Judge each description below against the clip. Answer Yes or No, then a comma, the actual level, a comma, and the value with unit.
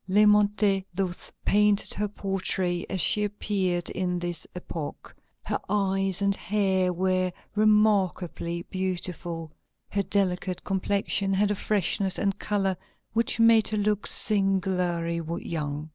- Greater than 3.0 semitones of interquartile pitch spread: No, narrow, 2.4 semitones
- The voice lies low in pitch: No, high, 195 Hz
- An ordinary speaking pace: No, slow, 120 wpm